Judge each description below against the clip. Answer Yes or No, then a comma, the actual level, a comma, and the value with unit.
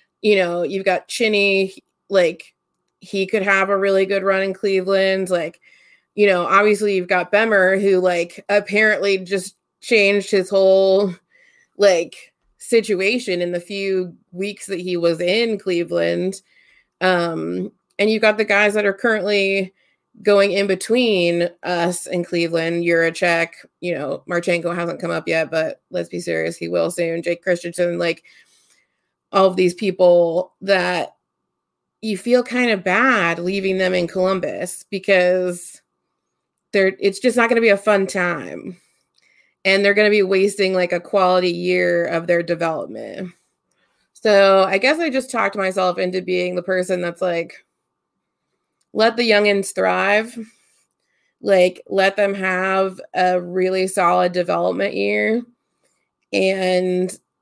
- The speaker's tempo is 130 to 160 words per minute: Yes, average, 145 wpm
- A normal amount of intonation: No, narrow, 2.3 semitones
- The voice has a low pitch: No, high, 190 Hz